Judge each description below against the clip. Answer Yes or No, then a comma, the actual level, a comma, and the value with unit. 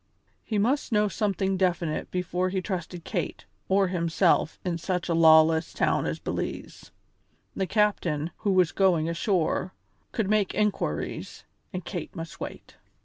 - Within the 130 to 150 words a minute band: Yes, average, 145 wpm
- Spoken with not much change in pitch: No, average, 3.0 semitones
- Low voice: No, medium, 185 Hz